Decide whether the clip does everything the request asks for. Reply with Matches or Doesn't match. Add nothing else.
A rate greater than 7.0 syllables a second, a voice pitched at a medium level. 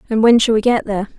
Doesn't match